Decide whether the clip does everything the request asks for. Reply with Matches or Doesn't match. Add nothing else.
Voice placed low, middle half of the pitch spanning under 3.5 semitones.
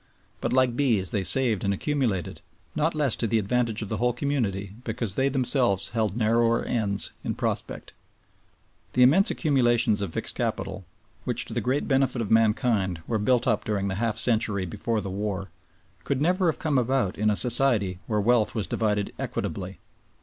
Doesn't match